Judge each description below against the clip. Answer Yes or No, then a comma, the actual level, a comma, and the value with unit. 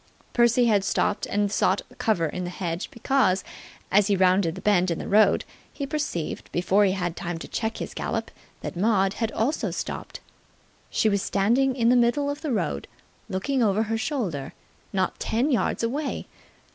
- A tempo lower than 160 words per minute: No, average, 180 wpm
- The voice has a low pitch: No, high, 210 Hz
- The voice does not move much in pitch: No, average, 4.2 semitones